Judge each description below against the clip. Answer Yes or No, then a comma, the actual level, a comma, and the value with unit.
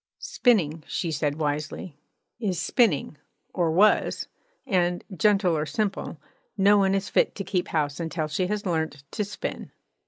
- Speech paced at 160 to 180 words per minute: No, average, 150 wpm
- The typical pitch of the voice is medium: Yes, medium, 175 Hz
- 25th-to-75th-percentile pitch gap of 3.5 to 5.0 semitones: Yes, average, 4.3 semitones